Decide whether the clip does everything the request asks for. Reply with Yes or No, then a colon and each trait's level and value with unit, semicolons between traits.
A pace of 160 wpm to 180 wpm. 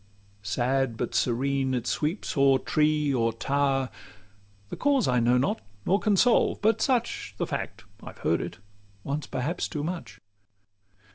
No: average, 150 wpm